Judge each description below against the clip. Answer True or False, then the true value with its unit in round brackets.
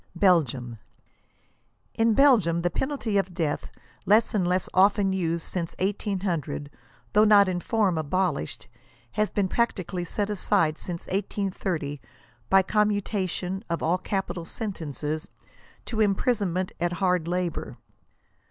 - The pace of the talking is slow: True (120 wpm)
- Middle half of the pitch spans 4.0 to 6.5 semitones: False (3.3 semitones)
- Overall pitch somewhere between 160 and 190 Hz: True (185 Hz)